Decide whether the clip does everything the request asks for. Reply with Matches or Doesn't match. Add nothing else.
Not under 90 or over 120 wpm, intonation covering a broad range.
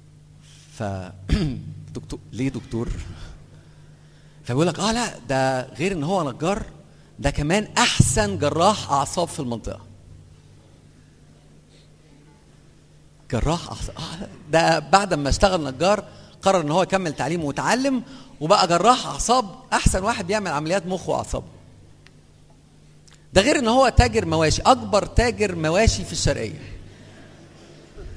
Matches